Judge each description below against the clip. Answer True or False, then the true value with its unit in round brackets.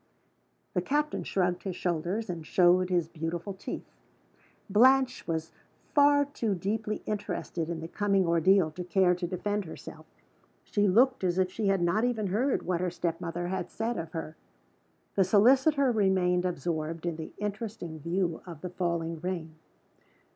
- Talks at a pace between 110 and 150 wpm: False (160 wpm)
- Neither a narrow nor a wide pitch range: True (3.5 semitones)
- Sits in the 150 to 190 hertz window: True (185 Hz)